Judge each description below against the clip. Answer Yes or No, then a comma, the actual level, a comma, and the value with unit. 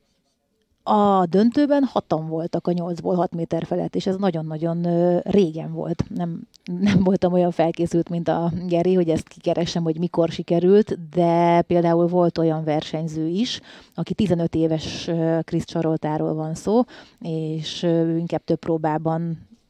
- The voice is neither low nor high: Yes, medium, 170 Hz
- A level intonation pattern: Yes, narrow, 1.7 semitones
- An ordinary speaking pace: Yes, average, 135 wpm